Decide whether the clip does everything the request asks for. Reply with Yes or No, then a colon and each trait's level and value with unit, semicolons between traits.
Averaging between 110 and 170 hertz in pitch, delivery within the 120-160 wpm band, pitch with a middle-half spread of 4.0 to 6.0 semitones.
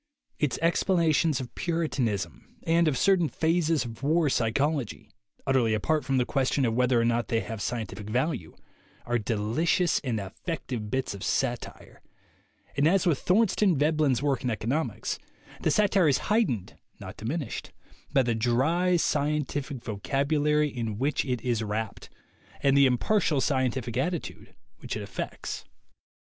Yes: low, 135 Hz; average, 145 wpm; average, 5.1 semitones